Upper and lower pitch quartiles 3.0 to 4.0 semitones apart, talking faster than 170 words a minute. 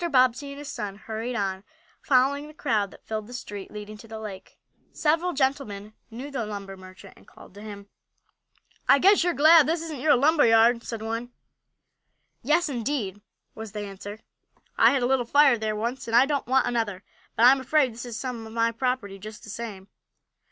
No: average, 4.5 semitones; average, 195 wpm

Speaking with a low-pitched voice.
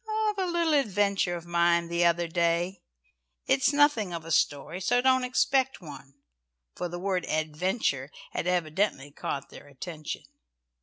No: medium, 175 Hz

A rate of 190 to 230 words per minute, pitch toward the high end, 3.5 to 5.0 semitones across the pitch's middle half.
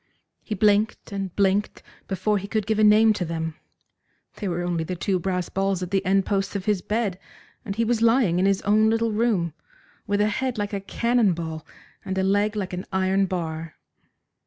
No: fast, 205 wpm; high, 195 Hz; average, 2.7 semitones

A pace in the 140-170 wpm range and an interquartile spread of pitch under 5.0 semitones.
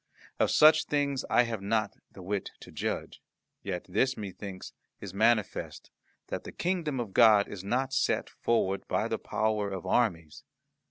Yes: average, 160 wpm; average, 4.4 semitones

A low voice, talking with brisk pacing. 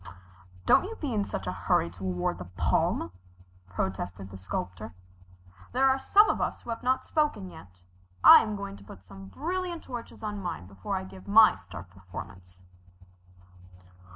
No: very low, 95 Hz; average, 170 wpm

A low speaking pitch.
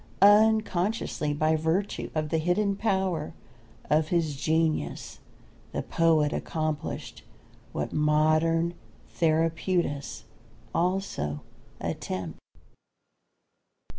No: medium, 160 Hz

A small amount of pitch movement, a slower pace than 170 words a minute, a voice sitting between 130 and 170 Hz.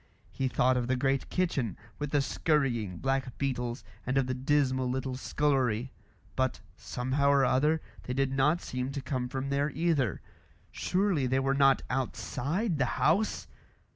Yes: narrow, 2.2 semitones; average, 160 wpm; low, 135 Hz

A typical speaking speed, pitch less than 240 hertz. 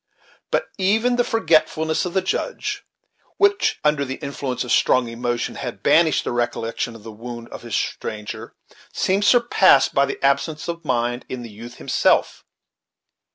Yes: average, 155 wpm; medium, 140 Hz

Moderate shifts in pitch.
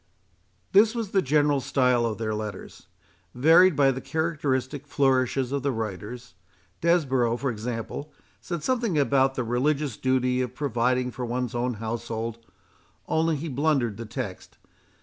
Yes: average, 3.9 semitones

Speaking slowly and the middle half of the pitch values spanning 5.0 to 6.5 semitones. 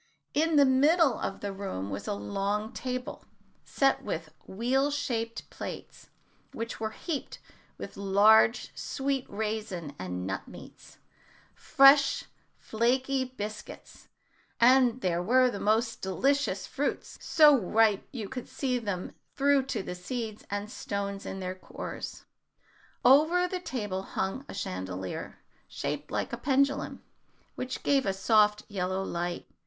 Yes: slow, 130 wpm; wide, 5.5 semitones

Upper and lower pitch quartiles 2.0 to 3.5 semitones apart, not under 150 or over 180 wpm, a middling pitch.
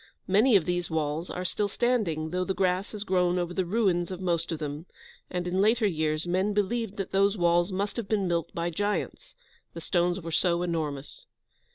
No: average, 2.8 semitones; average, 200 wpm; medium, 180 Hz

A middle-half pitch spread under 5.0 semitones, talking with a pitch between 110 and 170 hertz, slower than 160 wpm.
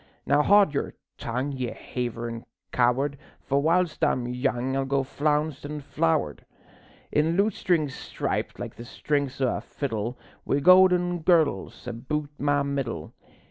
Yes: average, 3.6 semitones; medium, 140 Hz; average, 140 wpm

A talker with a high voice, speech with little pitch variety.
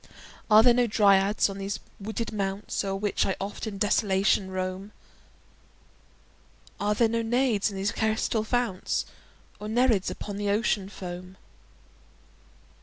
Yes: high, 205 Hz; narrow, 2.2 semitones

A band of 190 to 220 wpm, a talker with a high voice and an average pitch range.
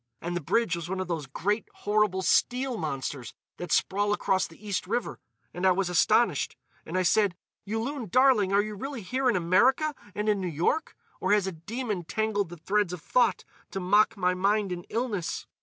Yes: average, 195 wpm; high, 200 Hz; average, 3.6 semitones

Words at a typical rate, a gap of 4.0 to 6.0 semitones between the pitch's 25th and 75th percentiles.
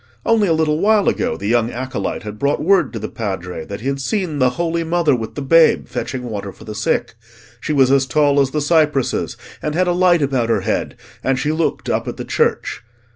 No: fast, 230 wpm; wide, 5.5 semitones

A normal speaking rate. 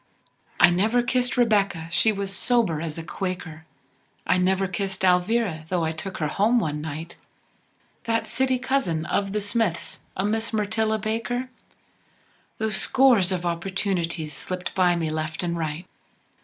Yes: average, 150 wpm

